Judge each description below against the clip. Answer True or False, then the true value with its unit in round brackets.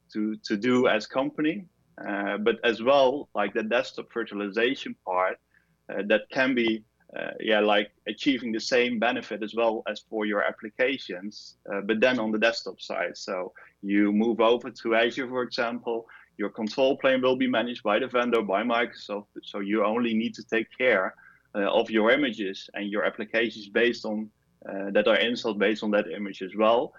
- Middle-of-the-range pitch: False (110 Hz)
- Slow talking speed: False (185 wpm)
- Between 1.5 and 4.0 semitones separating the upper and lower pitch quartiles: True (2.7 semitones)